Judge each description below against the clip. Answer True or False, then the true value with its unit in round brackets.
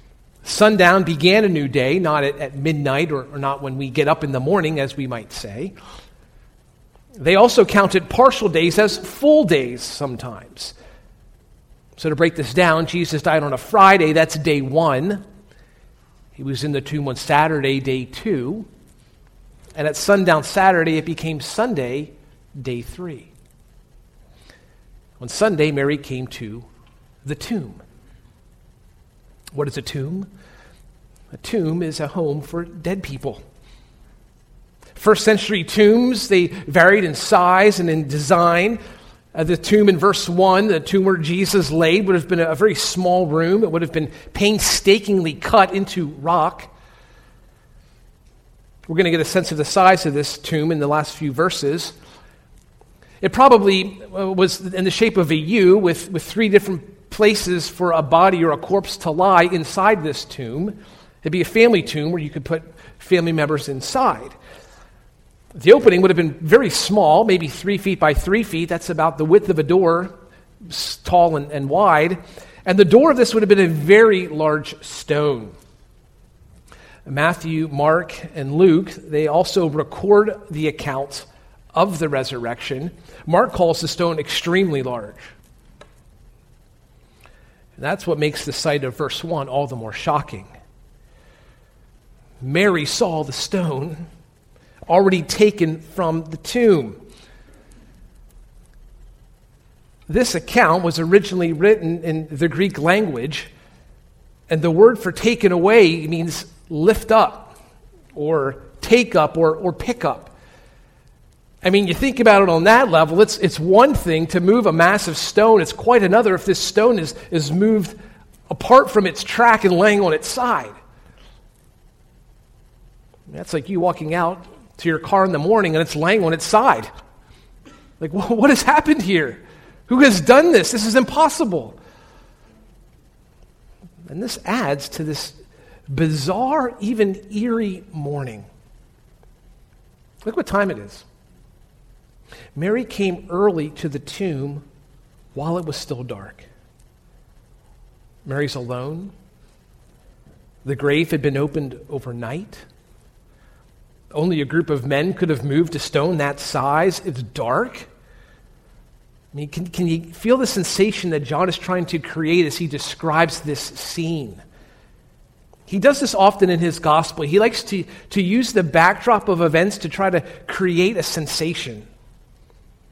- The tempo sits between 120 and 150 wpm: True (145 wpm)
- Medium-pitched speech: True (170 Hz)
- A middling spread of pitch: True (4.6 semitones)